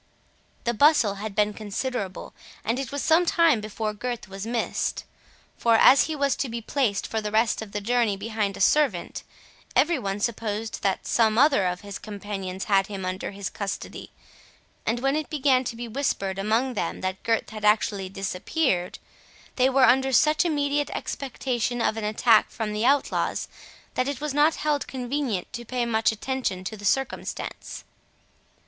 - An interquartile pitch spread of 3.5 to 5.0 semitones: Yes, average, 4.6 semitones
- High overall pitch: Yes, high, 225 Hz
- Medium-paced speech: Yes, average, 175 wpm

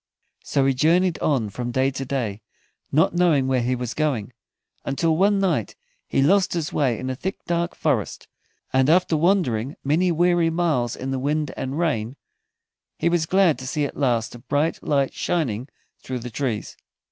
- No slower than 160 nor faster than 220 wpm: Yes, average, 180 wpm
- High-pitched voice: No, medium, 140 Hz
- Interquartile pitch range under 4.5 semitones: No, average, 4.9 semitones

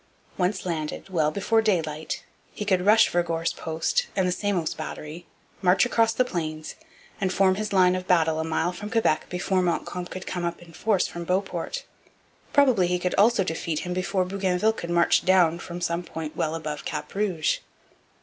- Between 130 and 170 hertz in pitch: No, medium, 180 Hz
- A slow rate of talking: No, average, 180 wpm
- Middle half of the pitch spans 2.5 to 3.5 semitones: Yes, average, 3.0 semitones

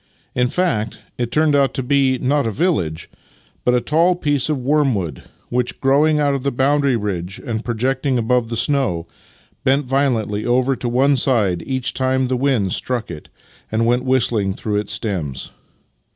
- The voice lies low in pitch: Yes, low, 125 Hz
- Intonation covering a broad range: No, average, 4.0 semitones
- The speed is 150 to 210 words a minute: Yes, average, 175 wpm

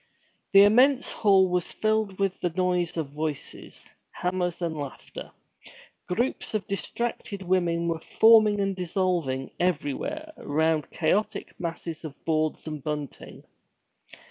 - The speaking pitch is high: No, medium, 180 Hz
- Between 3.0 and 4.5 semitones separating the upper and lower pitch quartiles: Yes, average, 4.0 semitones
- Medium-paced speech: No, slow, 120 wpm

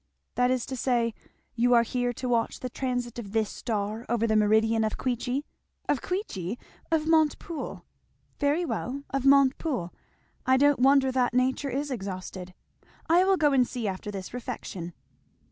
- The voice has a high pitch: Yes, high, 245 Hz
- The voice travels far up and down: No, average, 3.7 semitones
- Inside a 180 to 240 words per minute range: No, average, 160 wpm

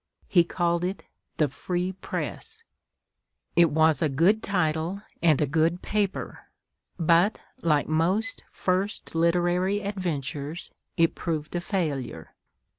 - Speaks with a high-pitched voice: No, medium, 170 Hz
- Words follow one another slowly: Yes, slow, 115 wpm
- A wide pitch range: No, average, 3.0 semitones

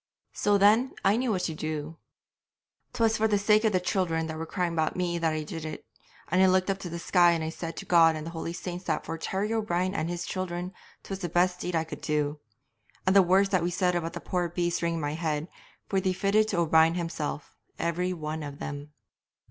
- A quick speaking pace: Yes, fast, 240 wpm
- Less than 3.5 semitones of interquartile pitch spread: Yes, average, 2.7 semitones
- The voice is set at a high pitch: No, medium, 175 Hz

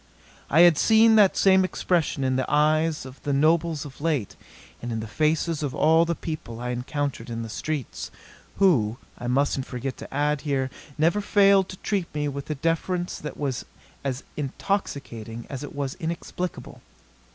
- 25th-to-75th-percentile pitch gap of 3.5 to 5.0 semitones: Yes, average, 4.3 semitones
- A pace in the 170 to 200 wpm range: Yes, average, 175 wpm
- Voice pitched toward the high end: No, medium, 150 Hz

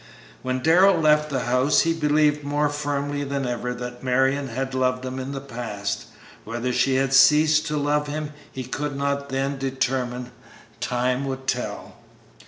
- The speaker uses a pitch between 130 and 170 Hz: Yes, low, 135 Hz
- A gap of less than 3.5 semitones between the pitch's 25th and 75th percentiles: Yes, narrow, 2.5 semitones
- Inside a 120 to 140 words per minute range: No, average, 165 wpm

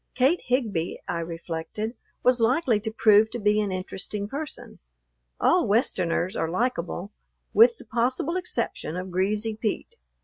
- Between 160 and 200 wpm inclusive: No, average, 140 wpm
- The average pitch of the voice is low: No, high, 215 Hz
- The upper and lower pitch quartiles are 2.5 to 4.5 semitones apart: No, average, 5.1 semitones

